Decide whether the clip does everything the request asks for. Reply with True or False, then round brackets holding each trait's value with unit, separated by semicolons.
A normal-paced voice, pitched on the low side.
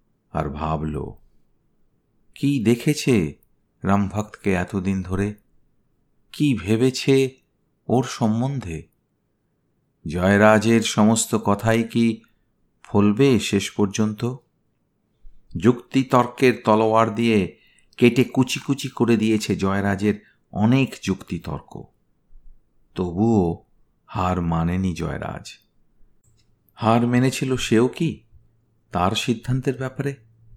True (80 wpm; 110 Hz)